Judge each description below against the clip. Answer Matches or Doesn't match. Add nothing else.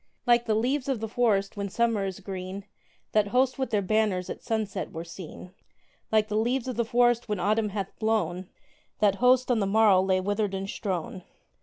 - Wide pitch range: Doesn't match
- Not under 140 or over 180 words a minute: Doesn't match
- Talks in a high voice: Matches